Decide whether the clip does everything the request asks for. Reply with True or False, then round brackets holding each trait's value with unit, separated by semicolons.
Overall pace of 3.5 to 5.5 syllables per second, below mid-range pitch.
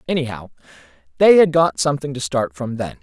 False (6.0 syllables/s; 125 Hz)